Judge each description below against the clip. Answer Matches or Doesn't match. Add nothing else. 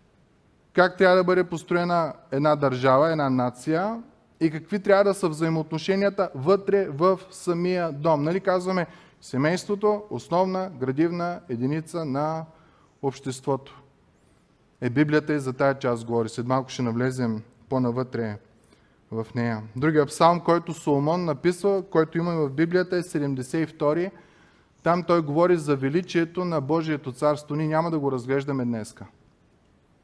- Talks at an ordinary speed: Matches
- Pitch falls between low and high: Matches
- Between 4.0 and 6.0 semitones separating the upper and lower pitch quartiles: Matches